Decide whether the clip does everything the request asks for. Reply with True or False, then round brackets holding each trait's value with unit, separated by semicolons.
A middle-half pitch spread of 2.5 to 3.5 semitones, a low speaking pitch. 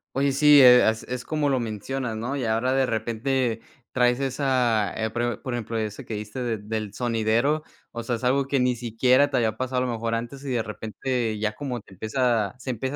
True (2.9 semitones; 120 Hz)